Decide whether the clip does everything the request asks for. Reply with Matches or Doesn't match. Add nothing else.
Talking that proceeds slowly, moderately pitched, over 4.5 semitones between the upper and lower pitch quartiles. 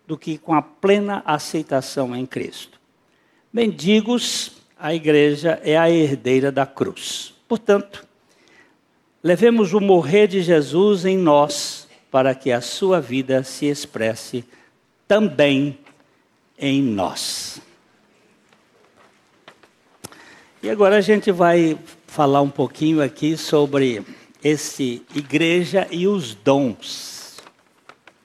Matches